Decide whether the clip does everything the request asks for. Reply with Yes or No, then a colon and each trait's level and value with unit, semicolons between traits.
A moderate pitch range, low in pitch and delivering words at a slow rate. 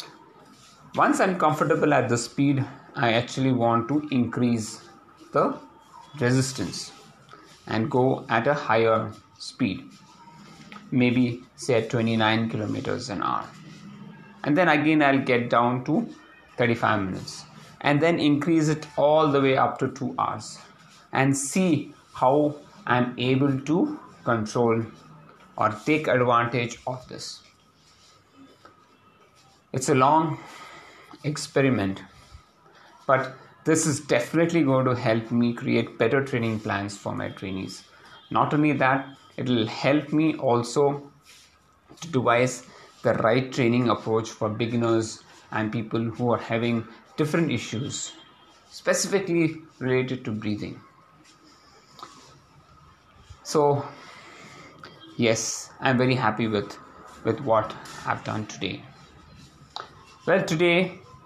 Yes: average, 4.5 semitones; low, 125 Hz; slow, 115 wpm